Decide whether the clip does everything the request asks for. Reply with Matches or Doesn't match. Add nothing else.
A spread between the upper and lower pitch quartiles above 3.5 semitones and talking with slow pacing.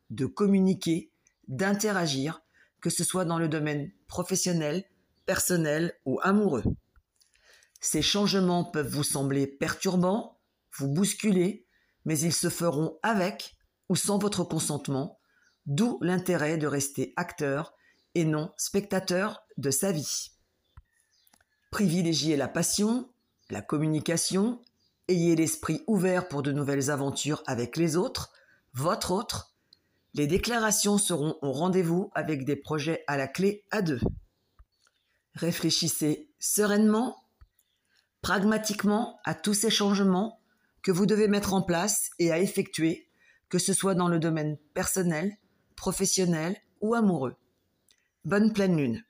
Matches